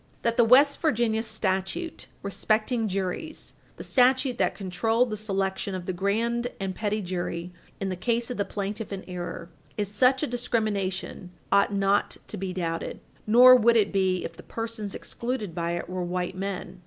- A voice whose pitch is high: Yes, high, 205 Hz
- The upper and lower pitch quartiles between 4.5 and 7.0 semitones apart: No, average, 3.9 semitones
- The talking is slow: No, average, 175 wpm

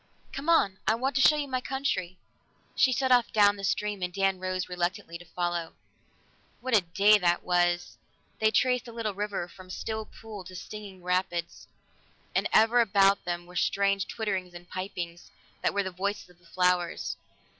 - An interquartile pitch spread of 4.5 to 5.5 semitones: No, average, 3.5 semitones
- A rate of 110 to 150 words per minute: No, average, 185 wpm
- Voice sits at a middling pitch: No, high, 195 Hz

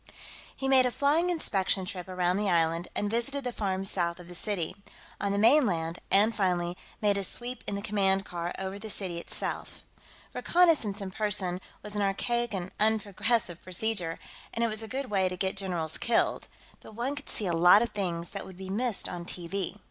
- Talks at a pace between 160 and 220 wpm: Yes, average, 200 wpm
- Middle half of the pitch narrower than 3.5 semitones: No, average, 3.8 semitones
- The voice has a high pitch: Yes, high, 200 Hz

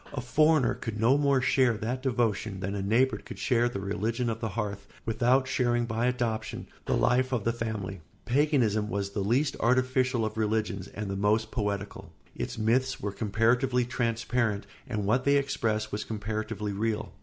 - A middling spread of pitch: Yes, average, 3.1 semitones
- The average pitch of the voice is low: Yes, low, 115 Hz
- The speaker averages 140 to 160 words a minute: No, average, 175 wpm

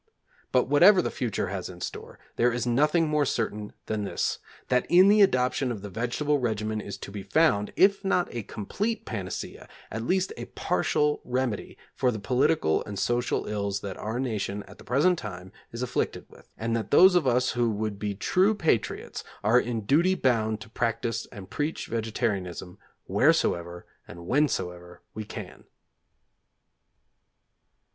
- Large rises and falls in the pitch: Yes, wide, 5.9 semitones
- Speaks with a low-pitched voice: Yes, low, 115 Hz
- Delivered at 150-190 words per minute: Yes, average, 165 wpm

